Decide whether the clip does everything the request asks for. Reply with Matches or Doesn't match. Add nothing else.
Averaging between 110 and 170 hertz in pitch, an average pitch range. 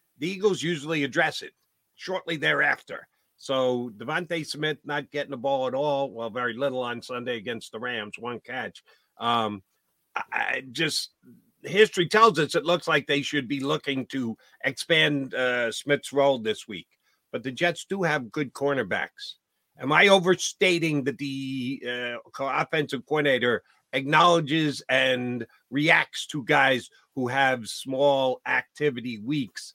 Matches